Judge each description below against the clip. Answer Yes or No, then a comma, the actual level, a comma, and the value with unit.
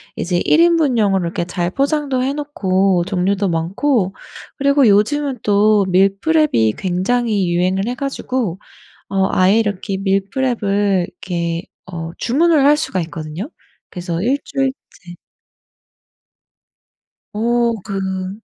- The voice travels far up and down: Yes, wide, 6.1 semitones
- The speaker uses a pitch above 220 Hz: No, high, 200 Hz